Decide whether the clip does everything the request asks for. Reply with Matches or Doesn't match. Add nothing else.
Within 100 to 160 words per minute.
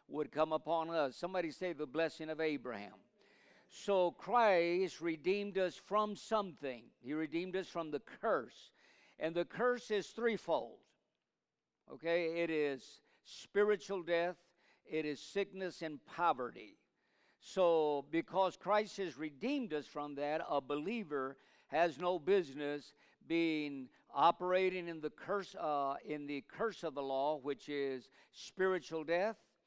Matches